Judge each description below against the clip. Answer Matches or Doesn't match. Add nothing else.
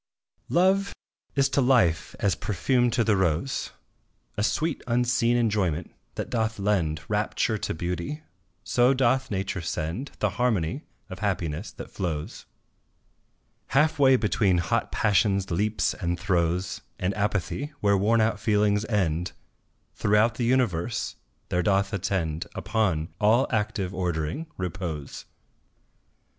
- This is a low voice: Matches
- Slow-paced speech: Matches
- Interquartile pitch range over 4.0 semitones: Matches